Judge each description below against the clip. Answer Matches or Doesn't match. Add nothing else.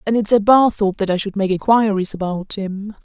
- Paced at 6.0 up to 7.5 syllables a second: Doesn't match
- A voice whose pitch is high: Matches